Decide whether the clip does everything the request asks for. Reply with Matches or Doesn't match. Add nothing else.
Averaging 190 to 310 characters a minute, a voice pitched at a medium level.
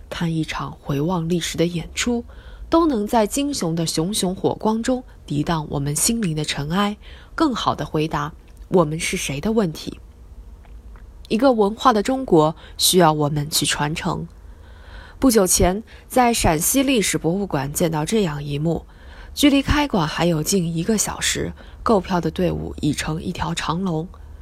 Matches